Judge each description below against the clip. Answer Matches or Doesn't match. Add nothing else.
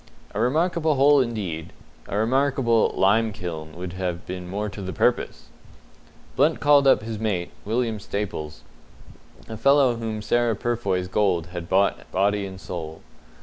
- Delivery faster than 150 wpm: Doesn't match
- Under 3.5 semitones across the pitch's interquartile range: Doesn't match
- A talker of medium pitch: Doesn't match